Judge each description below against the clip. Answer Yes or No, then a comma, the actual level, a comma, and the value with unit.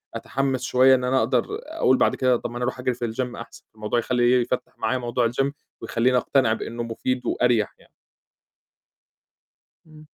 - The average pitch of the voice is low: Yes, low, 125 Hz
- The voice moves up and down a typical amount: No, narrow, 1.4 semitones